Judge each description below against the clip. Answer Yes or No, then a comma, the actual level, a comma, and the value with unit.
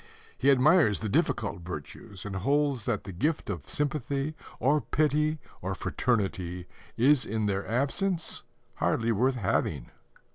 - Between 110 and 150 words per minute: Yes, slow, 135 wpm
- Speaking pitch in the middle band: No, low, 120 Hz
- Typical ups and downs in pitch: No, wide, 6.6 semitones